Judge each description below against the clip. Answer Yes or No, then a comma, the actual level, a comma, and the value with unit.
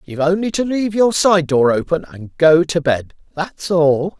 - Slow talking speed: No, average, 200 wpm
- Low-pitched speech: No, medium, 165 Hz